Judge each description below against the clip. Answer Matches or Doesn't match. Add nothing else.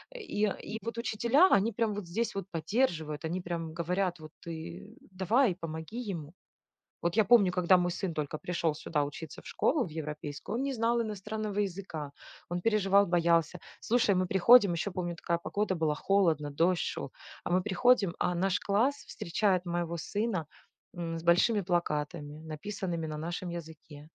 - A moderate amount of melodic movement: Matches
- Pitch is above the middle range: Doesn't match